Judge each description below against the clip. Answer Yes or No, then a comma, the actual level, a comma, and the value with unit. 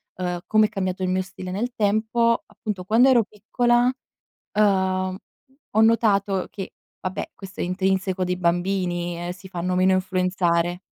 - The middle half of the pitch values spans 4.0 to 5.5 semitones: No, narrow, 2.6 semitones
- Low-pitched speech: No, high, 190 Hz